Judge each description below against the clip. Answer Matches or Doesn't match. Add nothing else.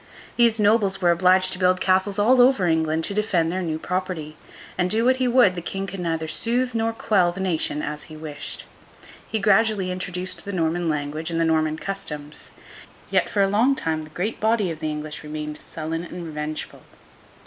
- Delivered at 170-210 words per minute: Matches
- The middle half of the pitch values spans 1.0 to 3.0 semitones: Doesn't match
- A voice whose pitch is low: Doesn't match